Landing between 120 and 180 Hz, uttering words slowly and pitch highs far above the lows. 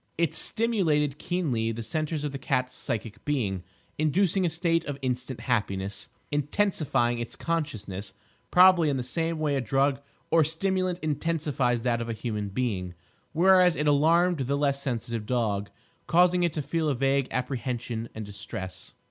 No: medium, 140 Hz; average, 155 wpm; wide, 5.8 semitones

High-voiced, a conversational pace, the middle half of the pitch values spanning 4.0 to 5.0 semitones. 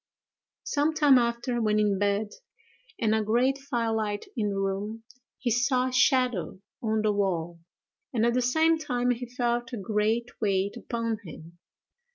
No: high, 230 Hz; average, 165 wpm; average, 3.2 semitones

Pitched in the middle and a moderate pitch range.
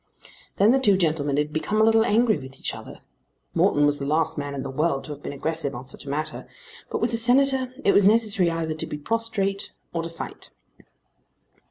No: medium, 165 Hz; wide, 7.0 semitones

